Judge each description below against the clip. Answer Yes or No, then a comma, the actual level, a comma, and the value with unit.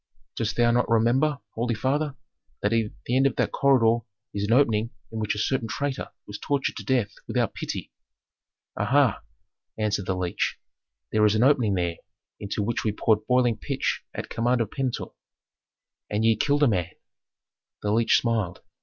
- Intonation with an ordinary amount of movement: Yes, average, 3.2 semitones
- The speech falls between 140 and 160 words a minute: No, average, 175 wpm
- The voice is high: No, low, 115 Hz